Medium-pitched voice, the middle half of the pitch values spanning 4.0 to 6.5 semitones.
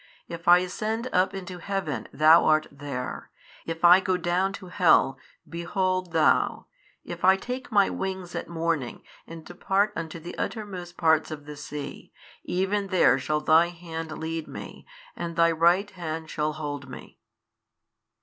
No: medium, 170 Hz; average, 3.1 semitones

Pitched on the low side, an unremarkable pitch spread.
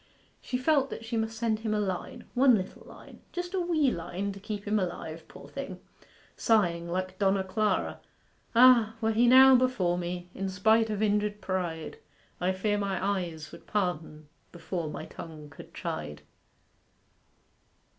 No: high, 200 Hz; average, 4.0 semitones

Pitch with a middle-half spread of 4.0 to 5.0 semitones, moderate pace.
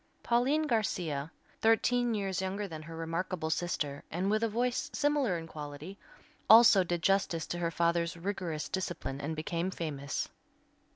Yes: average, 4.6 semitones; average, 150 wpm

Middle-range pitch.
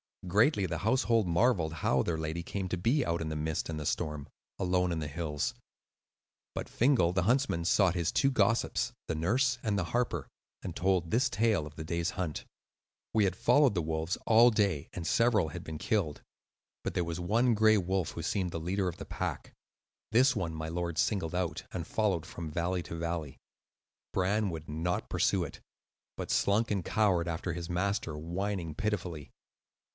No: very low, 90 Hz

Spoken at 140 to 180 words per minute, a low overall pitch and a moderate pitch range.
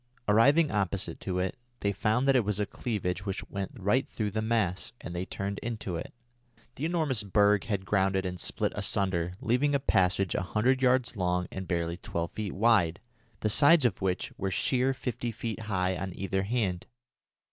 No: average, 190 wpm; low, 100 Hz; average, 4.1 semitones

